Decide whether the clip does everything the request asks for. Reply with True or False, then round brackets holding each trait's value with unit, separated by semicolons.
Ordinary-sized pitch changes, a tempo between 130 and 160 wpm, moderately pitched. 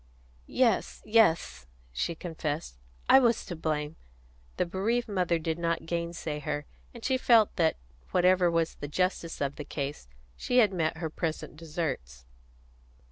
True (3.7 semitones; 145 wpm; 165 Hz)